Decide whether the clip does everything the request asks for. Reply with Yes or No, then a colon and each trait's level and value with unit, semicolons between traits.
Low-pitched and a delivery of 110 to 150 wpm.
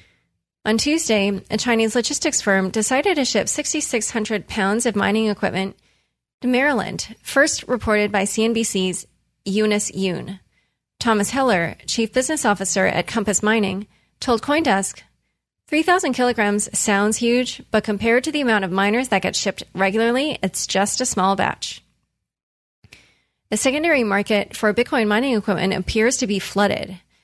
No: high, 215 Hz; average, 140 wpm